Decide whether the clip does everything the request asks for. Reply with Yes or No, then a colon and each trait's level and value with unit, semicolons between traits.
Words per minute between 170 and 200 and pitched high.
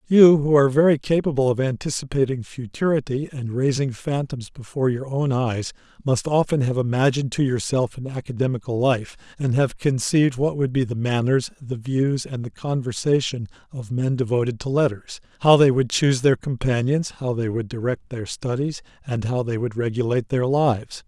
No: average, 175 wpm; low, 130 Hz